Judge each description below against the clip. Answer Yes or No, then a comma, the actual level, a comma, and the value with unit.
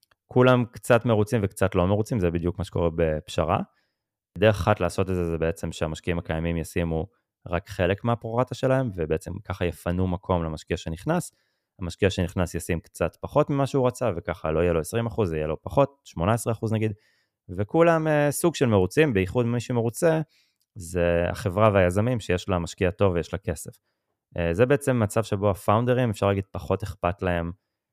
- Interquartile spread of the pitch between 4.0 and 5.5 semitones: Yes, average, 5.1 semitones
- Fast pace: Yes, fast, 165 wpm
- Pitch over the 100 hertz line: No, very low, 95 Hz